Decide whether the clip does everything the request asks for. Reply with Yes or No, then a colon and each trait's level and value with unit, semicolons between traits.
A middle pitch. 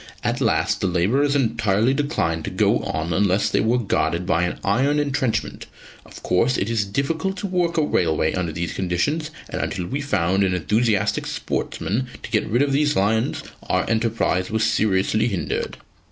No: low, 110 Hz